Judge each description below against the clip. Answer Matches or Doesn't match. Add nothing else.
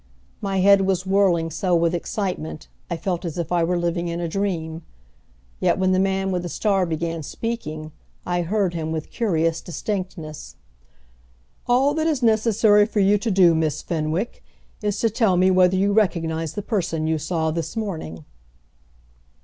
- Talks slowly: Doesn't match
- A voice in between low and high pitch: Matches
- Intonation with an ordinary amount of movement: Matches